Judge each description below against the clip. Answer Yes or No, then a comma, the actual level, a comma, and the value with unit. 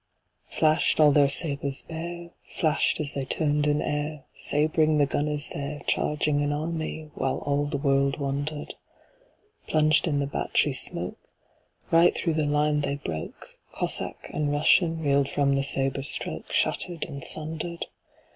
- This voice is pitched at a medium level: Yes, medium, 150 Hz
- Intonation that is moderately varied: No, narrow, 1.8 semitones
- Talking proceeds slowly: Yes, slow, 120 wpm